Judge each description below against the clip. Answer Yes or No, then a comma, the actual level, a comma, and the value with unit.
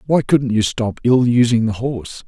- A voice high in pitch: No, low, 120 Hz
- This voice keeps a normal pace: No, fast, 210 wpm